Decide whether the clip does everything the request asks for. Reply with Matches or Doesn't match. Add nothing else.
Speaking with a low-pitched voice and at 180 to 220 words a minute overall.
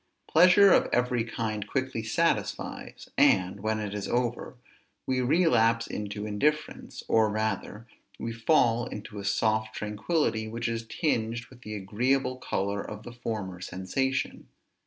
Doesn't match